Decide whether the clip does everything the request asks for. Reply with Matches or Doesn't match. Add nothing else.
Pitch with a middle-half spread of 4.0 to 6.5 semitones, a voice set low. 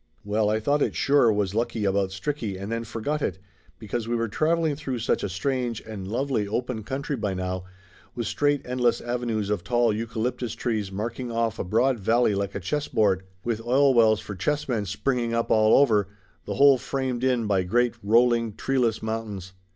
Doesn't match